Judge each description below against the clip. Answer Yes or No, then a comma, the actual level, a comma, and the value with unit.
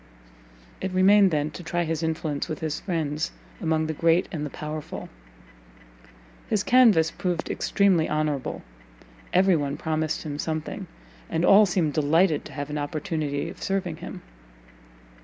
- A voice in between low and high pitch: Yes, medium, 160 Hz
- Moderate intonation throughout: Yes, average, 3.1 semitones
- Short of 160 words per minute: Yes, average, 140 wpm